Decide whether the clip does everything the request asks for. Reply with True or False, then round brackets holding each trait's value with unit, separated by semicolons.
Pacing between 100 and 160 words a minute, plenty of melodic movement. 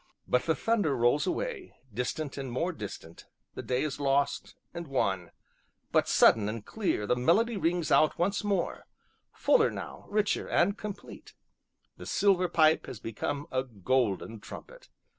True (150 wpm; 8.0 semitones)